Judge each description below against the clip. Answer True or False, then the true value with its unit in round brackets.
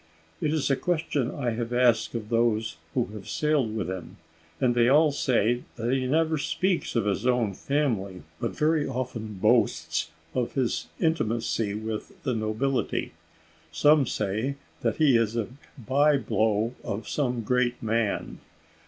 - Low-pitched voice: True (120 Hz)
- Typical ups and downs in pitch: True (4.1 semitones)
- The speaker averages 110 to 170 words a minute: True (155 wpm)